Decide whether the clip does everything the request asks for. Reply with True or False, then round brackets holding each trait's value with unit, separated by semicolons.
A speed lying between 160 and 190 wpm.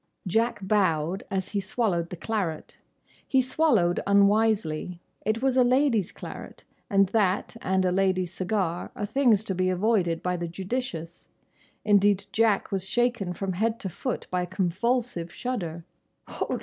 False (150 wpm)